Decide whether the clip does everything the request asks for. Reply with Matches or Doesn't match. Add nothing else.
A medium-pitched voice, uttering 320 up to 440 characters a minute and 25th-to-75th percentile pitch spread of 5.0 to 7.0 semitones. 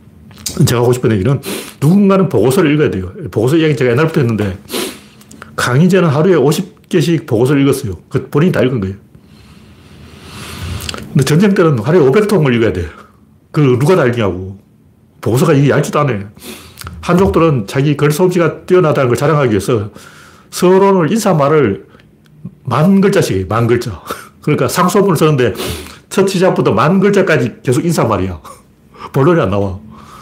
Doesn't match